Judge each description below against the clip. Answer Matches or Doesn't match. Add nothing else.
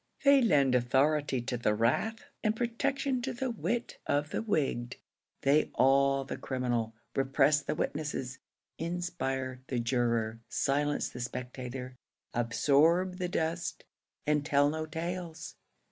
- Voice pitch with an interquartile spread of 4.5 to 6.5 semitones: Matches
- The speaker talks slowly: Matches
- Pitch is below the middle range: Doesn't match